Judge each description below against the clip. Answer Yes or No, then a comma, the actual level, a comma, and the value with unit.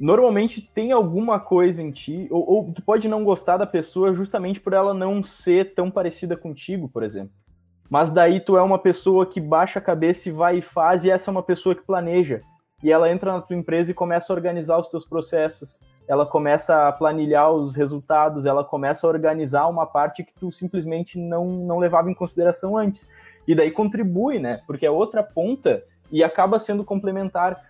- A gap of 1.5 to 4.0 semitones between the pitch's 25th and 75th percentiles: Yes, average, 3.2 semitones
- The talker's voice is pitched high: No, medium, 175 Hz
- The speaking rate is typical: No, fast, 195 wpm